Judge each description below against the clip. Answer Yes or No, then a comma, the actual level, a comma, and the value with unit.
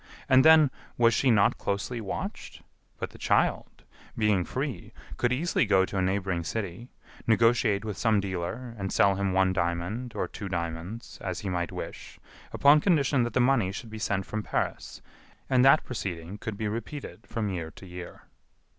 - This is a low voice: Yes, low, 105 Hz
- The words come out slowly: No, average, 175 wpm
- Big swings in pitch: No, average, 4.4 semitones